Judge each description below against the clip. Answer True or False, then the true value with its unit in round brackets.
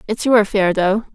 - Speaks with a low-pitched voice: False (210 Hz)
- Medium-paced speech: False (210 wpm)